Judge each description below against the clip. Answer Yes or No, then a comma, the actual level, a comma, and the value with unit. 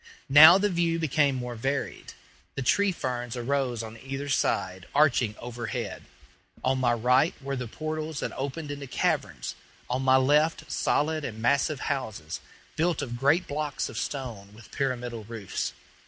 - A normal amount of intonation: Yes, average, 3.8 semitones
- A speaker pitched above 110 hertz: Yes, low, 135 Hz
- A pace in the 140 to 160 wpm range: Yes, average, 155 wpm